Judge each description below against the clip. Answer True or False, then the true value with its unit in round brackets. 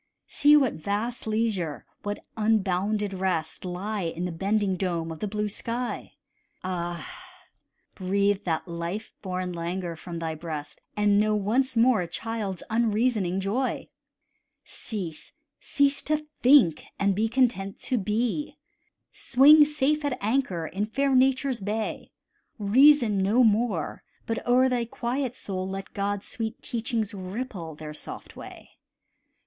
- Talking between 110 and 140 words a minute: True (135 wpm)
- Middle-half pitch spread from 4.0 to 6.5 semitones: True (4.7 semitones)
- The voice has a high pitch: True (210 Hz)